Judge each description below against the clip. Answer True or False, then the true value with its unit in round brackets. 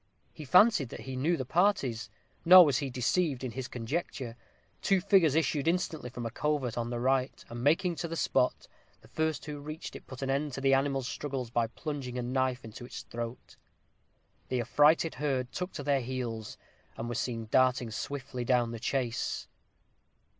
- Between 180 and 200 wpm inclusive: True (185 wpm)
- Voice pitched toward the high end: False (130 Hz)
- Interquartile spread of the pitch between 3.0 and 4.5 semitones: True (3.7 semitones)